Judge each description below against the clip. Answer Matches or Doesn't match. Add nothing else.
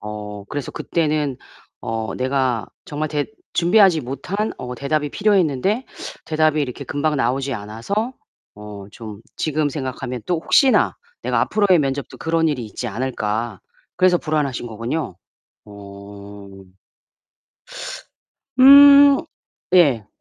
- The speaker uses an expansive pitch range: Matches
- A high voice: Doesn't match